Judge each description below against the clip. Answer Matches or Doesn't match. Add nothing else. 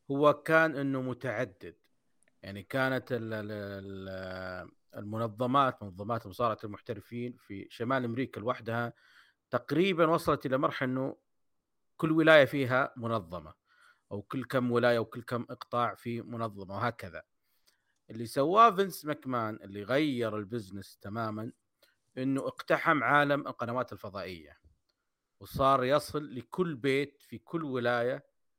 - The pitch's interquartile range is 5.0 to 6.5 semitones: Doesn't match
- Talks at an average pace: Matches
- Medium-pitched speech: Doesn't match